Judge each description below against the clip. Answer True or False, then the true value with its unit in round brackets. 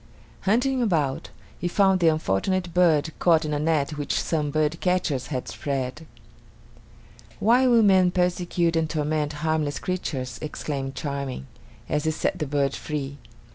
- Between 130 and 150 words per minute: True (140 wpm)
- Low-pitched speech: False (155 Hz)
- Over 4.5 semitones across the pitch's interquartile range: False (3.7 semitones)